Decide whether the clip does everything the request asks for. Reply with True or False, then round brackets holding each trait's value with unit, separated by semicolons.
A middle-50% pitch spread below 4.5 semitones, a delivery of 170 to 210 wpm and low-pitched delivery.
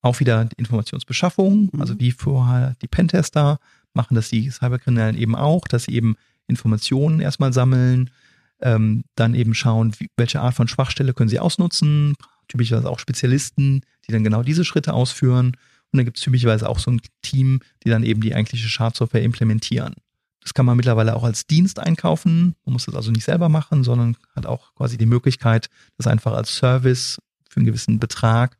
True (3.4 semitones; 185 wpm; 125 Hz)